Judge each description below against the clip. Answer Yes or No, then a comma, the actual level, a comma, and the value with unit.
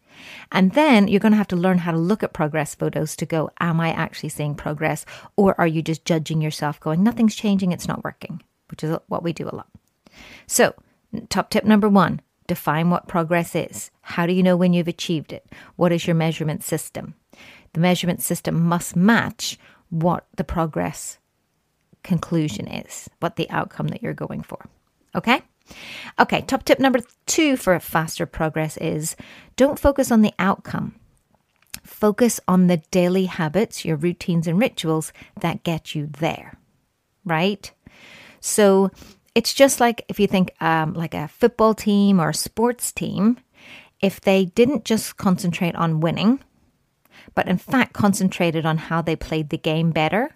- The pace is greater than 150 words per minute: Yes, average, 170 wpm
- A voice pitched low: No, medium, 175 Hz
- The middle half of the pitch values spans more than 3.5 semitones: Yes, average, 4.0 semitones